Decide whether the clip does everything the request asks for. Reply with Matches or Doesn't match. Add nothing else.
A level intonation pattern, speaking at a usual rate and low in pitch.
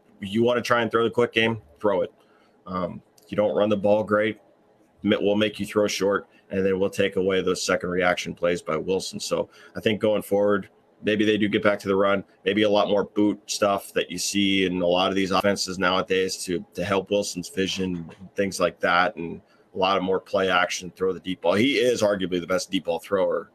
Doesn't match